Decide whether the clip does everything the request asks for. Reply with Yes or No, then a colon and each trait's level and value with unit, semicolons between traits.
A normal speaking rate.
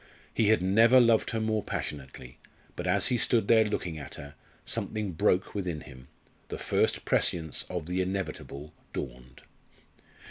Yes: average, 150 wpm